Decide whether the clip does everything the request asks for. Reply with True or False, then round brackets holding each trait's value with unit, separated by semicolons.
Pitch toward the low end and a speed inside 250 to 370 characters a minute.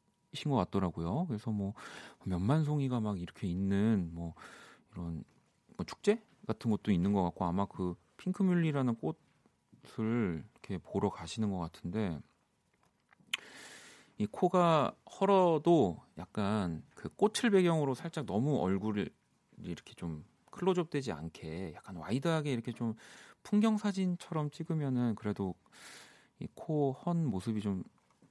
True (115 Hz; 265 characters per minute)